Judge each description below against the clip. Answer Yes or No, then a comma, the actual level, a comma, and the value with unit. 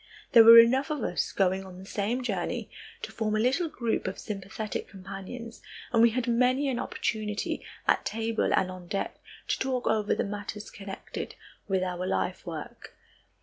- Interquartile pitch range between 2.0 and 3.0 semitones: No, average, 3.5 semitones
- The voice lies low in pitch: No, high, 215 Hz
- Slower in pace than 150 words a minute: No, average, 175 wpm